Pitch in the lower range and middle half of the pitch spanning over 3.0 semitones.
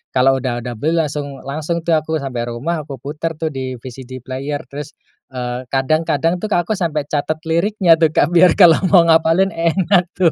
No: medium, 155 Hz; average, 4.0 semitones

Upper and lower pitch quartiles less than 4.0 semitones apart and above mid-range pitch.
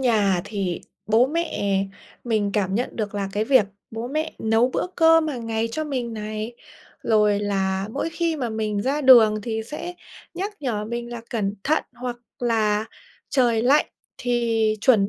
Yes: average, 3.5 semitones; high, 230 Hz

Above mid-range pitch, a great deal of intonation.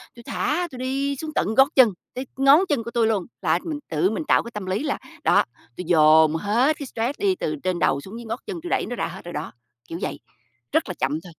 Yes: high, 235 Hz; wide, 7.6 semitones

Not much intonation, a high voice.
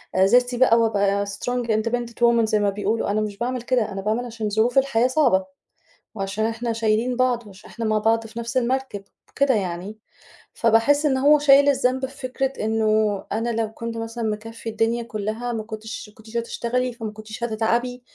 Yes: narrow, 2.3 semitones; high, 230 Hz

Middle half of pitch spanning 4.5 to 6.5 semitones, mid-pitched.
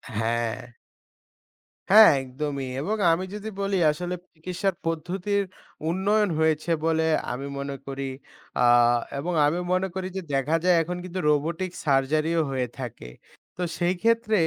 Yes: average, 5.2 semitones; medium, 165 Hz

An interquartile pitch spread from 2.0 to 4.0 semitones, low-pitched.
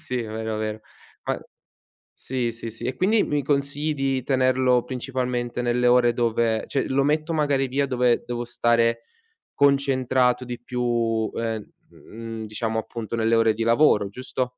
Yes: narrow, 2.4 semitones; low, 125 Hz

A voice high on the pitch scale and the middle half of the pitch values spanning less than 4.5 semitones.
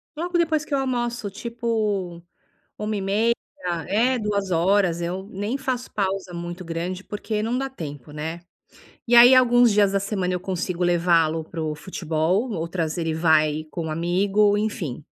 No: high, 195 Hz; average, 5.0 semitones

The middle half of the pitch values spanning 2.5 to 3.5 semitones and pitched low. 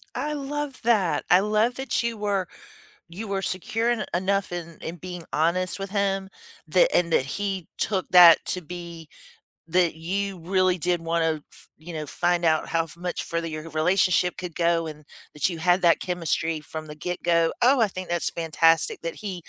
No: average, 2.9 semitones; medium, 175 Hz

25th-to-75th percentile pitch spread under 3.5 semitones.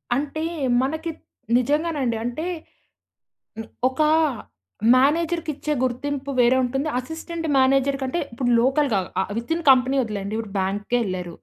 No: average, 4.0 semitones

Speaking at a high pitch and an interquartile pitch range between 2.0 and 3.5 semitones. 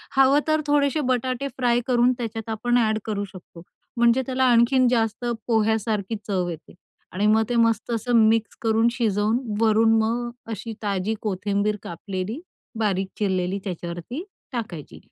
Yes: high, 225 Hz; average, 3.1 semitones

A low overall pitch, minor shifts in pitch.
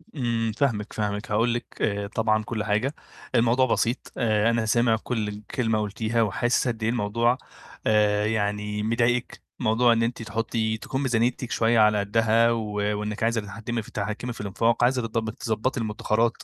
Yes: low, 115 Hz; narrow, 1.8 semitones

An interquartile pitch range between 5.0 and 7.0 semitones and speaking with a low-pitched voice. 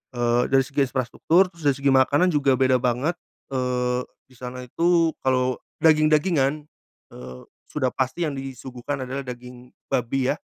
No: average, 2.7 semitones; low, 130 Hz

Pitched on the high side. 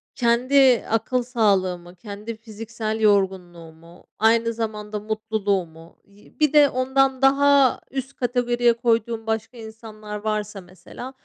Yes: high, 220 Hz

